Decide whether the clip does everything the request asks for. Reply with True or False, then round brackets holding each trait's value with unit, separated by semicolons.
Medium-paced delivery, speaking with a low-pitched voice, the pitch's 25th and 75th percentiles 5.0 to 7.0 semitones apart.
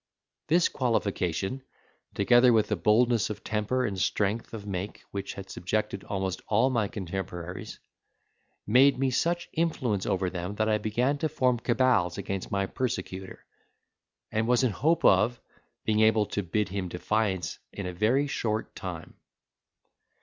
False (150 wpm; 105 Hz; 4.3 semitones)